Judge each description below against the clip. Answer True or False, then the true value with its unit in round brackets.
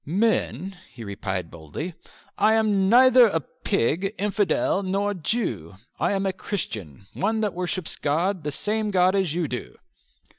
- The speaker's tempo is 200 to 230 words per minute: False (145 wpm)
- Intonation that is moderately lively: False (6.0 semitones)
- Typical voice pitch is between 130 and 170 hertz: False (190 Hz)